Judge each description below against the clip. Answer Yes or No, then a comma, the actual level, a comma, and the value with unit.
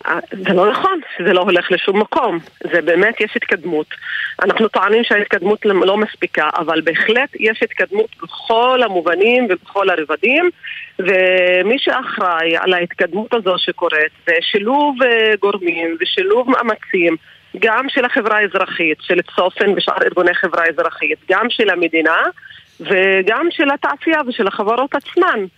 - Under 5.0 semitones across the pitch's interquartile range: No, average, 5.3 semitones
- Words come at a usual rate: Yes, average, 130 wpm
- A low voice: No, high, 200 Hz